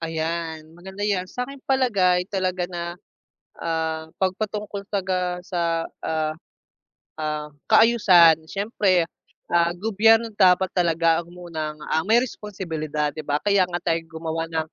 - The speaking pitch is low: No, medium, 175 Hz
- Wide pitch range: No, average, 3.5 semitones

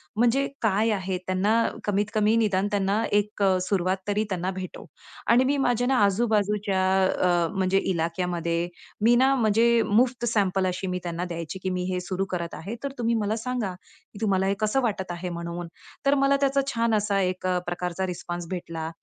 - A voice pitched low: No, high, 195 Hz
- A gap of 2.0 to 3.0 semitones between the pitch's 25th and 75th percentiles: No, average, 3.6 semitones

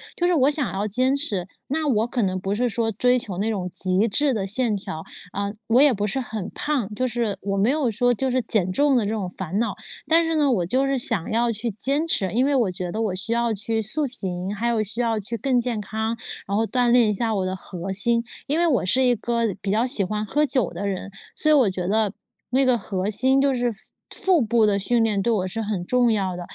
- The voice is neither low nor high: No, high, 225 Hz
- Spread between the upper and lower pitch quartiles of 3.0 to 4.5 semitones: Yes, average, 4.2 semitones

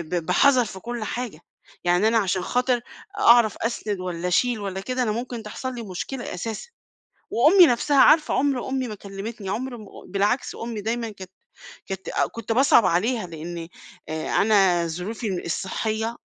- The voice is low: No, high, 220 Hz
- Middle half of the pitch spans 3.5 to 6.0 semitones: Yes, average, 4.3 semitones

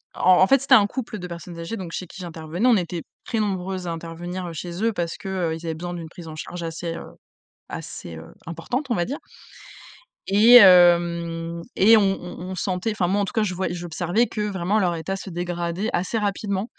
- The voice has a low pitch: No, medium, 180 Hz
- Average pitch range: Yes, average, 3.0 semitones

